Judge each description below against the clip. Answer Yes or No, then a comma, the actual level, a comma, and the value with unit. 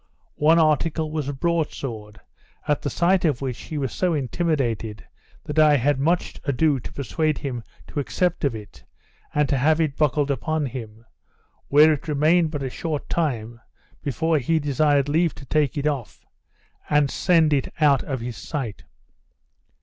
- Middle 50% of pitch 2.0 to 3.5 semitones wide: Yes, average, 3.0 semitones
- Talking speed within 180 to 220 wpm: No, average, 170 wpm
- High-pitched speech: No, medium, 145 Hz